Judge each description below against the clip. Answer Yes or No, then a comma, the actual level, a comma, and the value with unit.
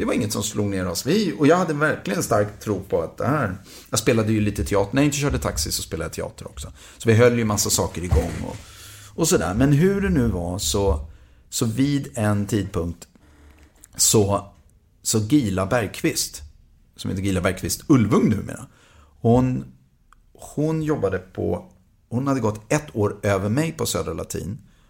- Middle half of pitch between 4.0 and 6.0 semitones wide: Yes, average, 5.1 semitones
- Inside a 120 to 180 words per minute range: No, average, 190 wpm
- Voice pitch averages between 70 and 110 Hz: Yes, low, 105 Hz